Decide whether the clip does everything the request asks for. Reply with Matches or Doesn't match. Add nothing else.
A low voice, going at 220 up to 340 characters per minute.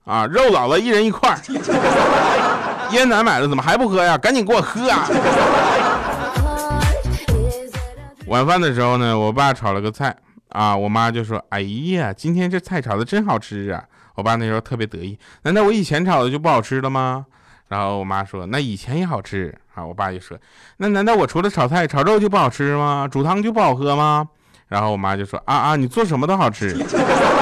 Matches